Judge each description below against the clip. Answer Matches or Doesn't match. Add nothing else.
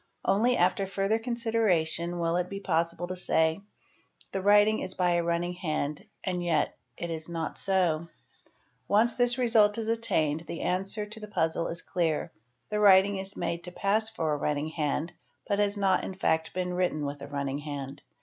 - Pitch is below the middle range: Doesn't match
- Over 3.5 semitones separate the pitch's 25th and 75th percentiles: Matches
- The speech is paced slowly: Doesn't match